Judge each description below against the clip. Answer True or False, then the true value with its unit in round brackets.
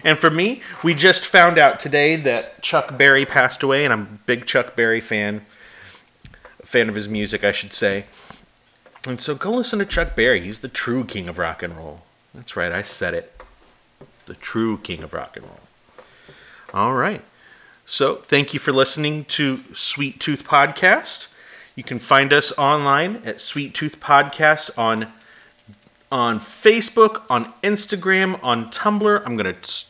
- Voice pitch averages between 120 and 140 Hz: True (135 Hz)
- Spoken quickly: False (170 wpm)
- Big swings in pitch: True (6.3 semitones)